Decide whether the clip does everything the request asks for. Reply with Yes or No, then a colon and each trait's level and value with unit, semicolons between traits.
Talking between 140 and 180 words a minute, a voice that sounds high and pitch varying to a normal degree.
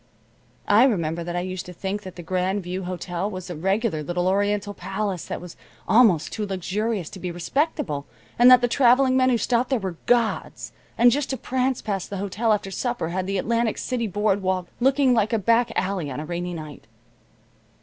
No: average, 200 wpm; high, 195 Hz; average, 4.7 semitones